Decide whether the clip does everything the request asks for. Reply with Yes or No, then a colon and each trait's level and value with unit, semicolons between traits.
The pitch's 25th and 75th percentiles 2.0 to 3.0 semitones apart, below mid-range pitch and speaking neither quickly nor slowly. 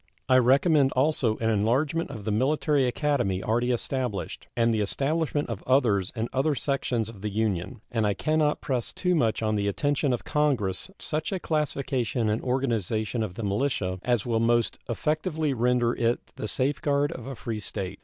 No: average, 4.6 semitones; low, 120 Hz; average, 180 wpm